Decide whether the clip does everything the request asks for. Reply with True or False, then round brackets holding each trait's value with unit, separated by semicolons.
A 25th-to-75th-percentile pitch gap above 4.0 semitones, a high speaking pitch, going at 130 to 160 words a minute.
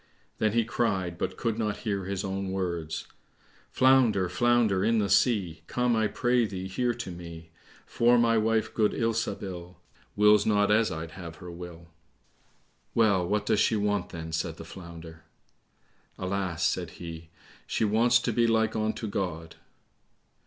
False (4.4 semitones; 100 Hz; 155 wpm)